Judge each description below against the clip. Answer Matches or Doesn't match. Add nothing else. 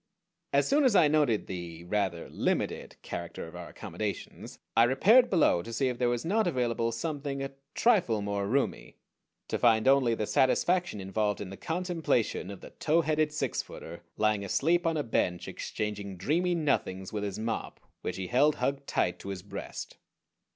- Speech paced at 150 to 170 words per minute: Doesn't match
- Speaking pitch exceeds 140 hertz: Doesn't match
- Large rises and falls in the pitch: Matches